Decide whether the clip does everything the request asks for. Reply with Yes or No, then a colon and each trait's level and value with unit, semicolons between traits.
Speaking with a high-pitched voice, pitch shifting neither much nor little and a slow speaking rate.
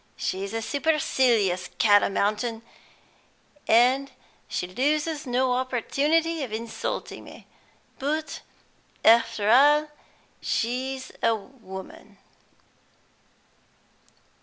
Yes: very high, 250 Hz; average, 4.3 semitones; slow, 85 wpm